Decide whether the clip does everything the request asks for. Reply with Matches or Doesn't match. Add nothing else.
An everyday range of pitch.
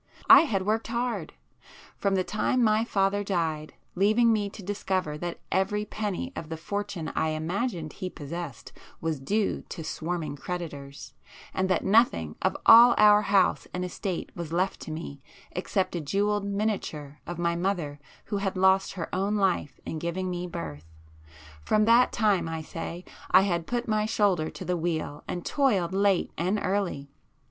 Matches